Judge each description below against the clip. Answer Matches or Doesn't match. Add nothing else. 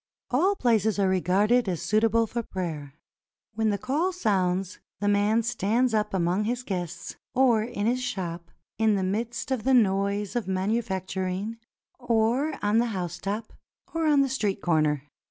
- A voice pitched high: Matches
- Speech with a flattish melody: Doesn't match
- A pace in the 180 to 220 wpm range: Doesn't match